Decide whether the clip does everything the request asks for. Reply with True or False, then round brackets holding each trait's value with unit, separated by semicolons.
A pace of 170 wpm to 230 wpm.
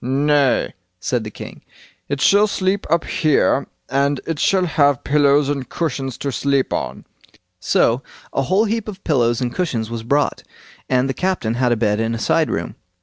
True (180 wpm)